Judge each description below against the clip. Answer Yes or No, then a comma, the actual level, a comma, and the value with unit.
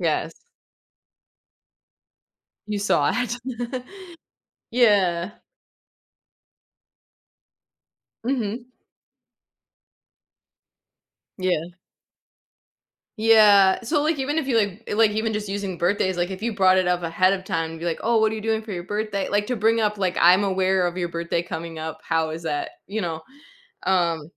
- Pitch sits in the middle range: No, high, 195 Hz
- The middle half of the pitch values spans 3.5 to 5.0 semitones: Yes, average, 4.0 semitones